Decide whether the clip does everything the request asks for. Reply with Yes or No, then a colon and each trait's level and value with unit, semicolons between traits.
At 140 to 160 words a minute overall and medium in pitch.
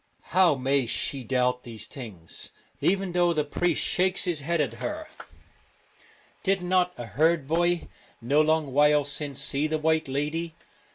Yes: average, 155 wpm; medium, 155 Hz